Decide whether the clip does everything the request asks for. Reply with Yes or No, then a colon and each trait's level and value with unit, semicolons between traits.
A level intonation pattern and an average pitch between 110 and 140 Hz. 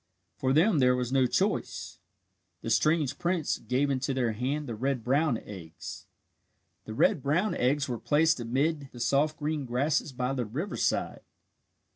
No: average, 3.5 semitones; low, 135 Hz